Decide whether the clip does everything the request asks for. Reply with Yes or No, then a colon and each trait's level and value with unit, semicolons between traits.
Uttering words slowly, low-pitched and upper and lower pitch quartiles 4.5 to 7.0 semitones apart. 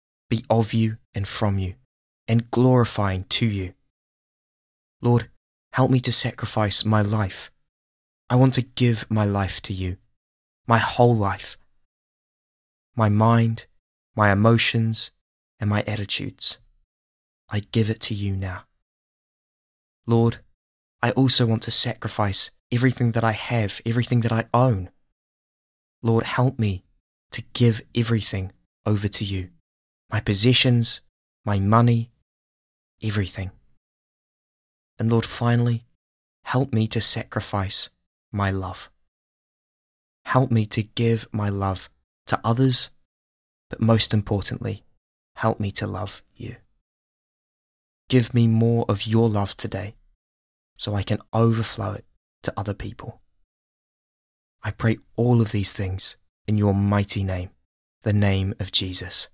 Yes: slow, 125 wpm; low, 105 Hz; average, 5.2 semitones